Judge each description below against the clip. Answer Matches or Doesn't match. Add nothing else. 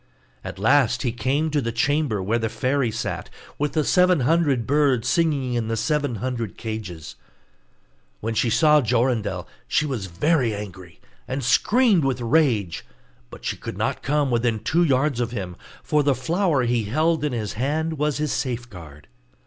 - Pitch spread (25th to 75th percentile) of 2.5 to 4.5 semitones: Doesn't match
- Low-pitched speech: Matches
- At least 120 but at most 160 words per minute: Doesn't match